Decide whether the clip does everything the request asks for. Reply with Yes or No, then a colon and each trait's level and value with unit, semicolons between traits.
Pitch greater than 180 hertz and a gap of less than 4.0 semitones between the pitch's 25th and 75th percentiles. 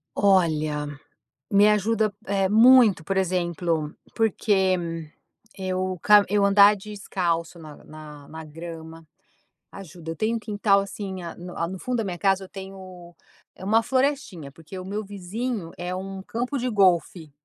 Yes: high, 190 Hz; average, 3.4 semitones